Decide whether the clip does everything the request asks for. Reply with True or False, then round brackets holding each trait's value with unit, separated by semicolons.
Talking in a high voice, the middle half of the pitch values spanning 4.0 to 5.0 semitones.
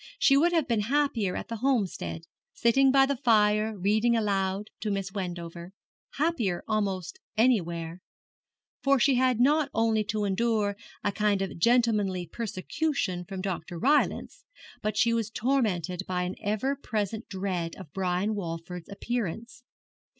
True (210 Hz; 4.4 semitones)